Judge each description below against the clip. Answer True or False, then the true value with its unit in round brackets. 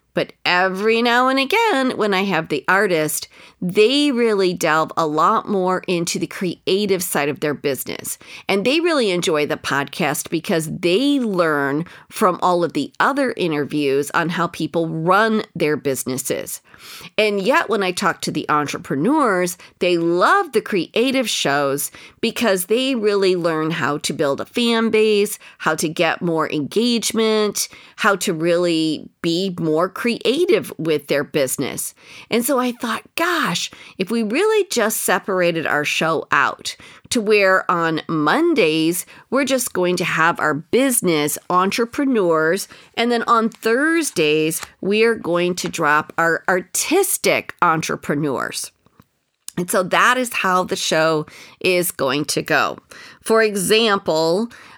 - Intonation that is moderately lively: False (5.9 semitones)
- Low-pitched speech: False (185 Hz)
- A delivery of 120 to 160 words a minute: True (145 wpm)